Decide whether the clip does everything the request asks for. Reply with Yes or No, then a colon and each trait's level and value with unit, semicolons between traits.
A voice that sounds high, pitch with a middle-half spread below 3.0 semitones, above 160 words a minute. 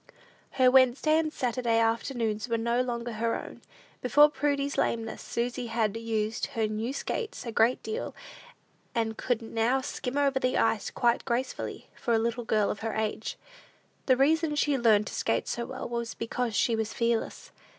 Yes: high, 235 Hz; narrow, 2.6 semitones; average, 175 wpm